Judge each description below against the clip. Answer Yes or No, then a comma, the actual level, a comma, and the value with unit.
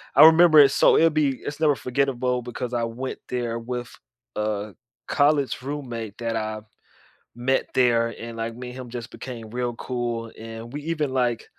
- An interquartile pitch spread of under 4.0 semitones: Yes, average, 2.8 semitones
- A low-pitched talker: Yes, low, 125 Hz